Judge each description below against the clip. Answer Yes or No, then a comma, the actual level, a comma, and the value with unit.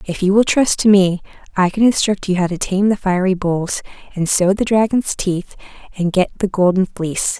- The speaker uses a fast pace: Yes, fast, 210 wpm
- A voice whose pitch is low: No, high, 190 Hz